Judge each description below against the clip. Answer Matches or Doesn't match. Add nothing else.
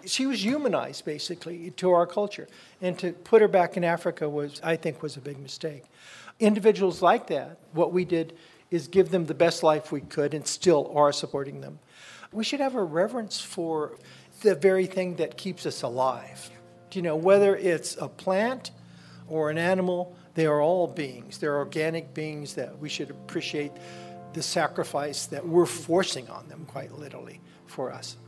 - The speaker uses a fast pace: Doesn't match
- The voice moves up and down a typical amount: Matches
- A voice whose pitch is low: Doesn't match